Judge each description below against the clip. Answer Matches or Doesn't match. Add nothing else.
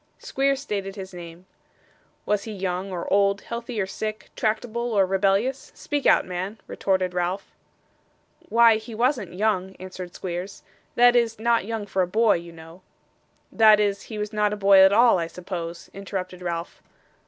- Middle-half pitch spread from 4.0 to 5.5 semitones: Doesn't match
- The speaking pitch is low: Doesn't match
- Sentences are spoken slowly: Doesn't match